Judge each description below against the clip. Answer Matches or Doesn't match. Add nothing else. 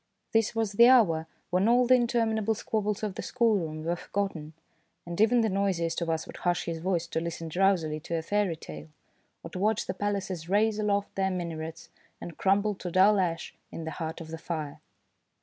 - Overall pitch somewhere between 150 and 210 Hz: Matches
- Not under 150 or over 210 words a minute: Matches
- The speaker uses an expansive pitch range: Doesn't match